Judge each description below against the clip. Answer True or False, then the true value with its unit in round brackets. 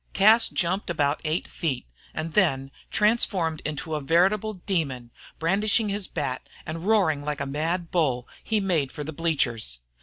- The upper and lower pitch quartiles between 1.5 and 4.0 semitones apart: False (5.1 semitones)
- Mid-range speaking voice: True (165 Hz)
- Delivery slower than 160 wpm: True (150 wpm)